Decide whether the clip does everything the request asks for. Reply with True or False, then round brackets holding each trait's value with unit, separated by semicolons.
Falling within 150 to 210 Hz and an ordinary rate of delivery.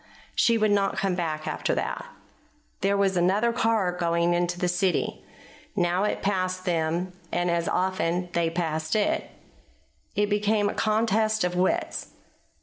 True (185 Hz; 145 wpm)